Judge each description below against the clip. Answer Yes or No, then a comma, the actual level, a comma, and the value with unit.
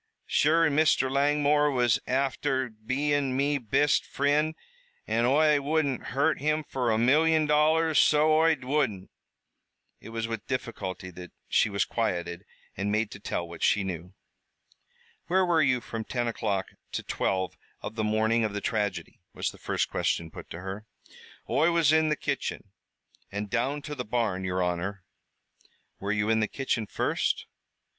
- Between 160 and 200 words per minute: Yes, average, 165 wpm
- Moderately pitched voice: No, low, 125 Hz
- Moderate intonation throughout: No, wide, 6.3 semitones